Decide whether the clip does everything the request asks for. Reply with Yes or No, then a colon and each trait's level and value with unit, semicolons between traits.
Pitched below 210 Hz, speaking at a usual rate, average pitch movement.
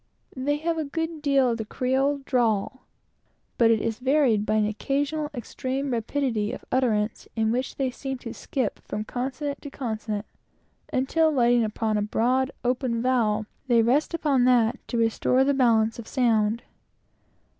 No: very high, 250 Hz; average, 160 wpm; average, 3.5 semitones